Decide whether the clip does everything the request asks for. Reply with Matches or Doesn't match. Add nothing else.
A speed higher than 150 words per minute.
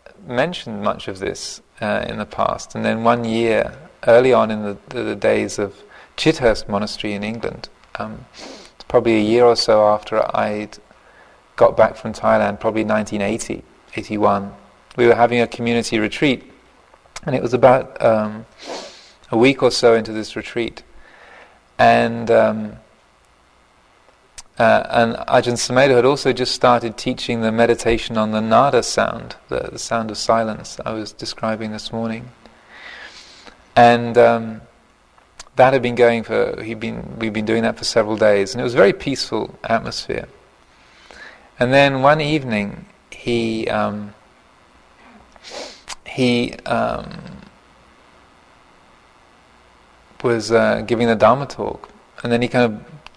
Doesn't match